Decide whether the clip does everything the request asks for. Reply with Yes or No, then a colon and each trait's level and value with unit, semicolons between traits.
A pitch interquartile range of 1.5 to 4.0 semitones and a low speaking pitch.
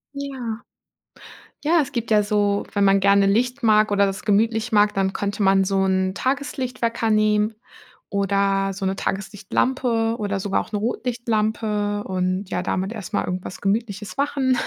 No: average, 2.7 semitones; high, 210 Hz